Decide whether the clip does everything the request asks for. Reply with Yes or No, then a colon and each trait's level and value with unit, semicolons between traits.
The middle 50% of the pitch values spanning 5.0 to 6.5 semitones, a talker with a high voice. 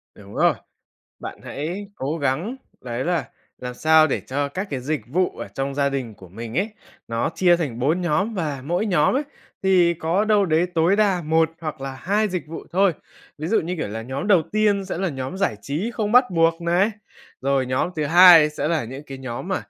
No: wide, 5.4 semitones; medium, 160 Hz